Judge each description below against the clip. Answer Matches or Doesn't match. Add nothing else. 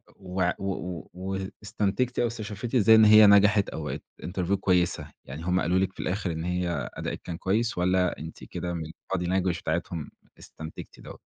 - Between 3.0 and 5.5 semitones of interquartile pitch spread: Doesn't match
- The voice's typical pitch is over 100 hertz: Doesn't match